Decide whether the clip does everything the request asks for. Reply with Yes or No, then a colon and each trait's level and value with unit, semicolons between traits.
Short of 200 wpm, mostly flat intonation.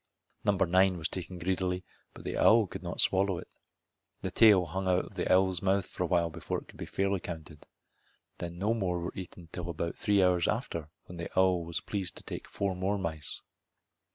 No: fast, 205 wpm; narrow, 2.1 semitones